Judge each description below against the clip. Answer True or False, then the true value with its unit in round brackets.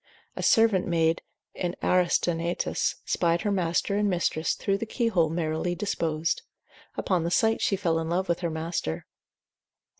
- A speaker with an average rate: True (155 wpm)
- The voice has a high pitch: False (175 Hz)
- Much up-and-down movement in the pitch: False (3.1 semitones)